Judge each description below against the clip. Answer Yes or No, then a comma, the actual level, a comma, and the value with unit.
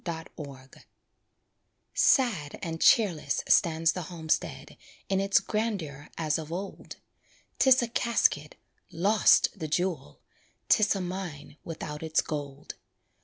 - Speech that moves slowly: Yes, slow, 120 wpm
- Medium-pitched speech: Yes, medium, 165 Hz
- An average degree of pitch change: Yes, average, 4.4 semitones